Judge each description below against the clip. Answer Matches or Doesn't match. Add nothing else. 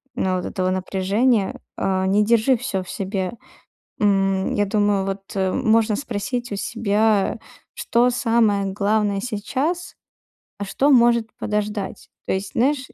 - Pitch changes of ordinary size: Matches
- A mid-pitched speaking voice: Doesn't match